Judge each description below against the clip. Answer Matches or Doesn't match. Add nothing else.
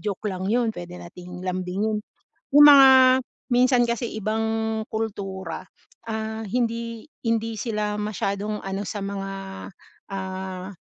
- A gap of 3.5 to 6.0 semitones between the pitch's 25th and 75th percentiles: Doesn't match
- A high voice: Matches